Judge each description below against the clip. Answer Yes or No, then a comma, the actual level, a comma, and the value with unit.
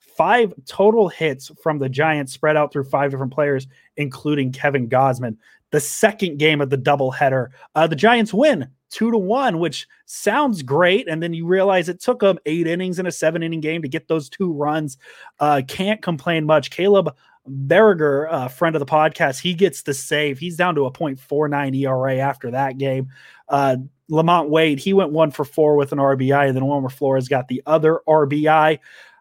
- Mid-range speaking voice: Yes, medium, 155 Hz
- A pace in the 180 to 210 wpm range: Yes, average, 190 wpm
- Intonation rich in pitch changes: No, average, 4.1 semitones